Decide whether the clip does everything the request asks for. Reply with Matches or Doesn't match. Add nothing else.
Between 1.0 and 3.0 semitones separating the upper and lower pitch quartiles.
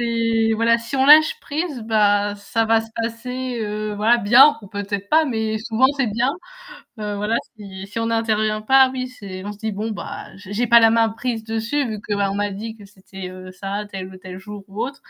Matches